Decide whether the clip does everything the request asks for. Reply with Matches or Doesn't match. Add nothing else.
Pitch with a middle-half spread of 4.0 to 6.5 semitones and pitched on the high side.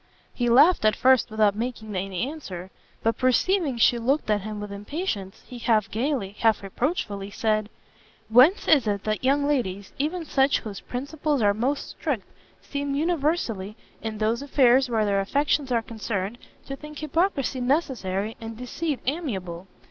Matches